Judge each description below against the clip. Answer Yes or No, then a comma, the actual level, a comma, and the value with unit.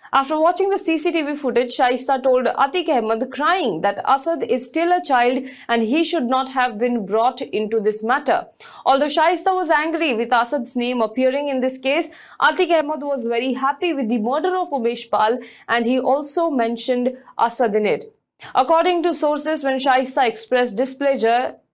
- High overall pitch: Yes, very high, 265 Hz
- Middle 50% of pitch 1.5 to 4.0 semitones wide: No, average, 4.7 semitones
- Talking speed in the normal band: Yes, average, 170 wpm